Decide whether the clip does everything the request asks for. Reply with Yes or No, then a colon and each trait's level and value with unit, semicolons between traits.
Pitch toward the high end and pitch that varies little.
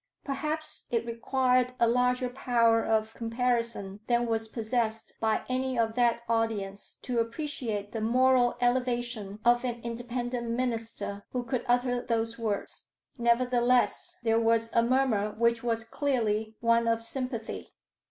Yes: high, 235 Hz; narrow, 1.6 semitones